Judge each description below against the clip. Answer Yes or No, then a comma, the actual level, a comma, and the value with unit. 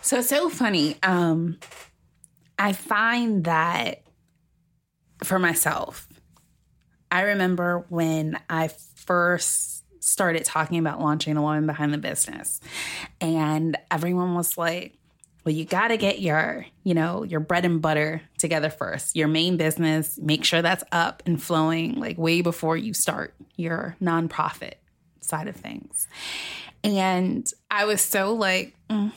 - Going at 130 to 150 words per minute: Yes, slow, 135 wpm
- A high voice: No, medium, 170 Hz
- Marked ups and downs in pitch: No, average, 3.1 semitones